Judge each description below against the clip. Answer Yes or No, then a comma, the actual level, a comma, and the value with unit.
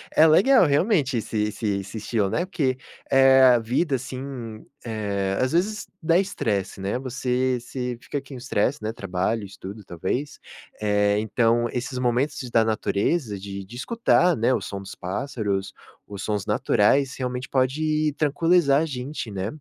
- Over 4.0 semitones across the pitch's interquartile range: Yes, average, 5.1 semitones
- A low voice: Yes, low, 125 Hz